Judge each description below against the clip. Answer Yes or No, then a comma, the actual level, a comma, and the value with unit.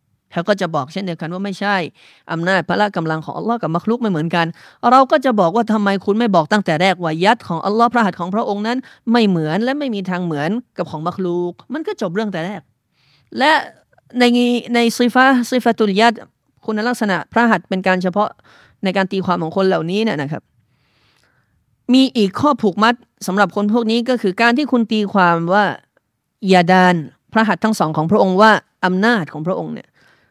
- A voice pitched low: No, high, 205 Hz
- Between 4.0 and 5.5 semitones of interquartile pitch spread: Yes, average, 4.7 semitones